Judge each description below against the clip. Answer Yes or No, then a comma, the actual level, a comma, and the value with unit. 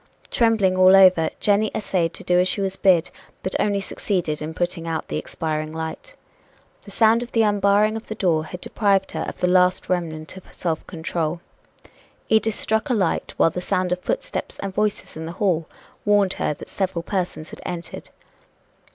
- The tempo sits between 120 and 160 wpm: No, average, 185 wpm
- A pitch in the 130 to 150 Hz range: No, medium, 185 Hz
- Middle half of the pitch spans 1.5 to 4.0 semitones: Yes, average, 3.6 semitones